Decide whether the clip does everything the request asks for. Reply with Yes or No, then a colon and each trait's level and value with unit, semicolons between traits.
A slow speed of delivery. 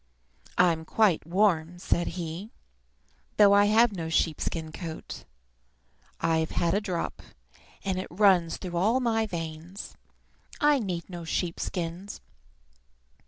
Yes: slow, 130 wpm